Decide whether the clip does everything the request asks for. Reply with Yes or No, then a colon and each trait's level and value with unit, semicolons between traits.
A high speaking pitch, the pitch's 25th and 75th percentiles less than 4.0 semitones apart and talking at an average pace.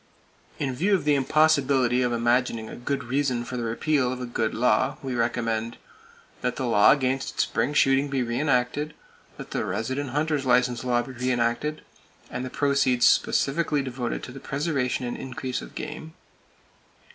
No: low, 130 Hz; narrow, 2.6 semitones; average, 170 wpm